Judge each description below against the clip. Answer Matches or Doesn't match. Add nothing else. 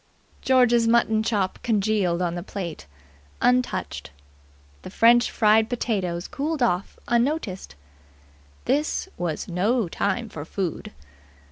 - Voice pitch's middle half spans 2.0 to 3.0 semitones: Doesn't match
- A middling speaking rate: Doesn't match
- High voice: Matches